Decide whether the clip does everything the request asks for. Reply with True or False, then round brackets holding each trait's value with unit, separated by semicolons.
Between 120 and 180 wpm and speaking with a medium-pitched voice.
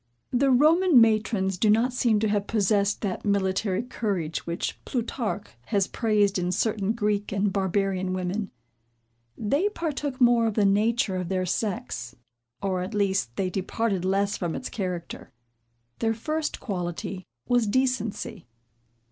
False (140 wpm; 205 Hz)